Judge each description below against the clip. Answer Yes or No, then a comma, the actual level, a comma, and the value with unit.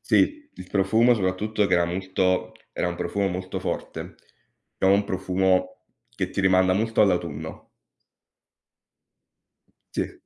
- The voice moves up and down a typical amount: No, narrow, 1.7 semitones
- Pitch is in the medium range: No, very low, 95 Hz